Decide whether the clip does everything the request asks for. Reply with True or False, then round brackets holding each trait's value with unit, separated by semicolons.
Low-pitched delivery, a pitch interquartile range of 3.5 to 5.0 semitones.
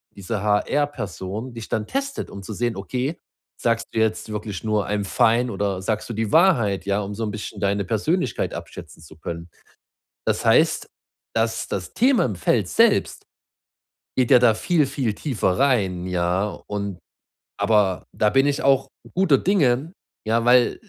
True (110 Hz; 4.2 semitones)